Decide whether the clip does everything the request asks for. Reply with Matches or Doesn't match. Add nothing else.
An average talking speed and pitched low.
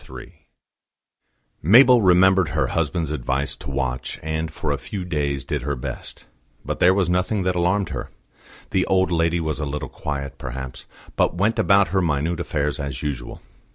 Matches